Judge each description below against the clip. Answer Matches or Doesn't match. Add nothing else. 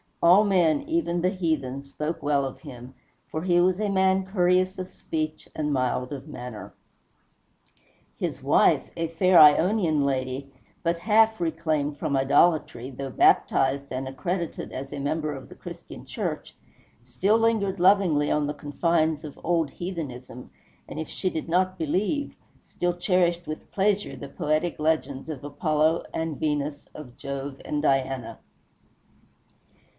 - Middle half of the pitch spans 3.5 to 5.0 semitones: Matches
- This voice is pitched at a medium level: Matches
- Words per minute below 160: Matches